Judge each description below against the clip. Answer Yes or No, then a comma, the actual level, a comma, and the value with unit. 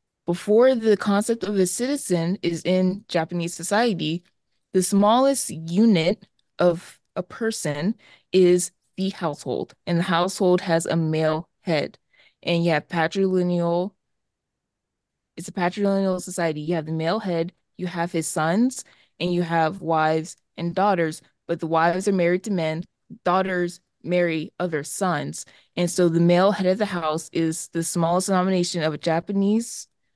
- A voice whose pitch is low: No, medium, 175 Hz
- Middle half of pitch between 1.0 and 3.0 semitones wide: Yes, average, 2.7 semitones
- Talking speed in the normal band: Yes, average, 150 wpm